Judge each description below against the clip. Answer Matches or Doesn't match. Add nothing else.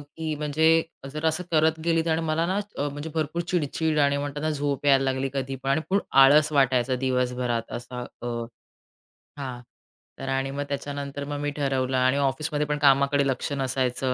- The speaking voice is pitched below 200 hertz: Matches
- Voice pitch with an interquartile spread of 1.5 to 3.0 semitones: Matches